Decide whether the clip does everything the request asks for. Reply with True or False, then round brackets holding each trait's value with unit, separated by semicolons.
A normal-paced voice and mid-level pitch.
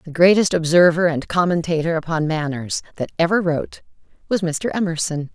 True (145 wpm; 165 Hz)